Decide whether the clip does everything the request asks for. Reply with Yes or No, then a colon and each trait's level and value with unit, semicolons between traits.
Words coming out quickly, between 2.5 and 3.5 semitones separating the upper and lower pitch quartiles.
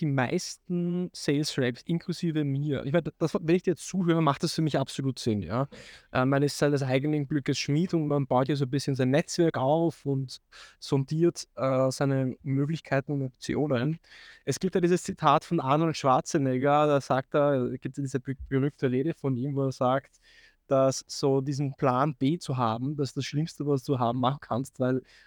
Yes: fast, 200 wpm; average, 2.8 semitones